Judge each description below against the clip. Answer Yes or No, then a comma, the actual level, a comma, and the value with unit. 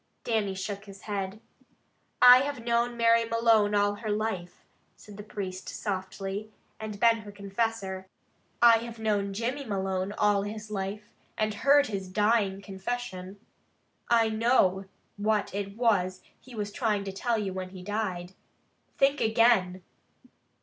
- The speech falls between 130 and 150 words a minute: Yes, average, 145 wpm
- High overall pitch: Yes, high, 210 Hz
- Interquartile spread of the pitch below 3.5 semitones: Yes, average, 2.8 semitones